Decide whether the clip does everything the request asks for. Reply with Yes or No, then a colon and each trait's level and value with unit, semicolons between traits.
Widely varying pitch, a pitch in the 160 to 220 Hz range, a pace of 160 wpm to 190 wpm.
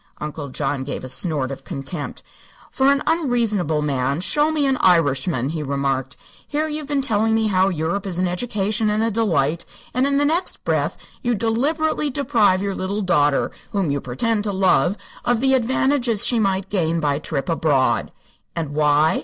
Yes: wide, 8.2 semitones; high, 190 Hz; average, 180 wpm